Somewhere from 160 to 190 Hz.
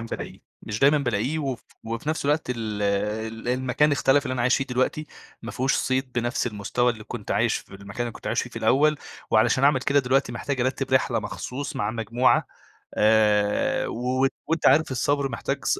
No: low, 125 Hz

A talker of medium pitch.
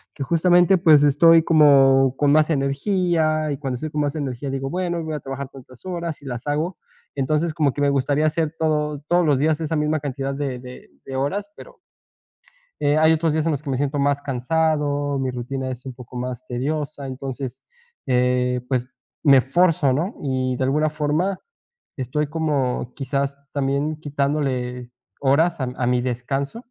Yes: medium, 145 Hz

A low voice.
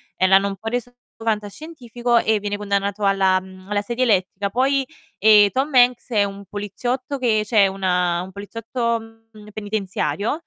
No: high, 210 Hz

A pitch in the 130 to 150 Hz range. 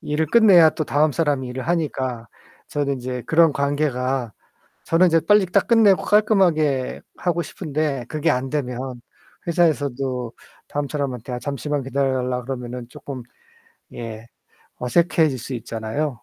Yes: medium, 140 Hz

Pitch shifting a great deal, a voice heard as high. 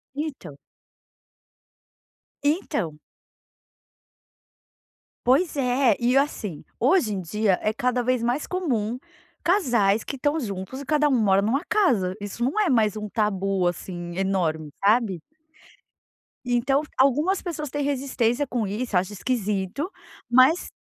Yes: wide, 6.0 semitones; high, 240 Hz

